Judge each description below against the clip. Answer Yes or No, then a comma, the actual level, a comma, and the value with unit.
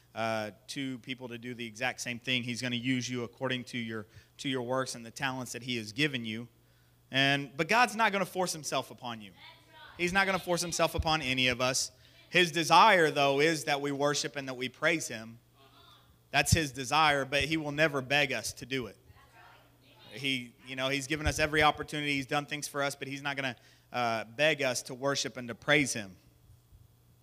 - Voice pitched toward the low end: Yes, low, 130 Hz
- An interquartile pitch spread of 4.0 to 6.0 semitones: No, average, 3.3 semitones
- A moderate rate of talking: No, fast, 220 wpm